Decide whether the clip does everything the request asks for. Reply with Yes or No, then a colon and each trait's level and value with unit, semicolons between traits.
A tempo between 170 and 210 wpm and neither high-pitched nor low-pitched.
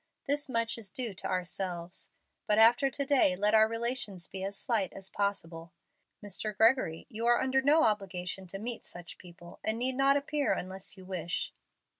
No: average, 180 wpm; high, 210 Hz